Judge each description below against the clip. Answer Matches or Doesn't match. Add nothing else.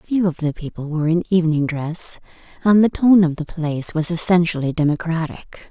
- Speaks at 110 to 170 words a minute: Doesn't match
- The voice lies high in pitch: Doesn't match